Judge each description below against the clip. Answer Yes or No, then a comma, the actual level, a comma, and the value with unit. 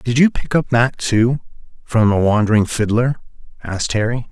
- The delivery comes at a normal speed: Yes, average, 165 wpm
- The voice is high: No, low, 115 Hz